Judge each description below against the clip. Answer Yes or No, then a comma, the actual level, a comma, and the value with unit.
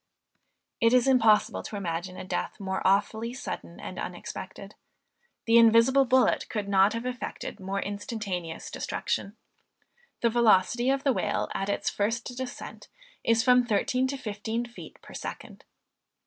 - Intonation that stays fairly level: No, average, 3.6 semitones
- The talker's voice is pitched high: Yes, high, 230 Hz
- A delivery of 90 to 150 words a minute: Yes, average, 145 wpm